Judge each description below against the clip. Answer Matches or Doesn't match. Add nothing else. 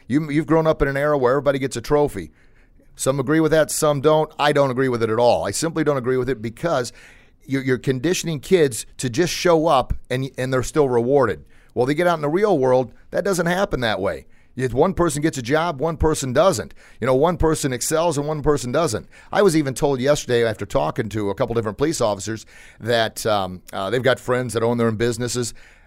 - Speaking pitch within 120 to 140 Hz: Matches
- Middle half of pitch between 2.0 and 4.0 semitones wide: Doesn't match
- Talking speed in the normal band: Doesn't match